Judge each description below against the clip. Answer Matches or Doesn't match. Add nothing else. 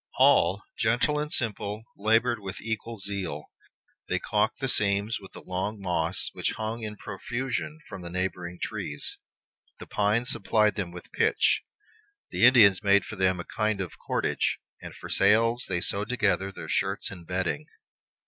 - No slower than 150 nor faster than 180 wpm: Matches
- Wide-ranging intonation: Doesn't match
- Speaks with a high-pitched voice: Doesn't match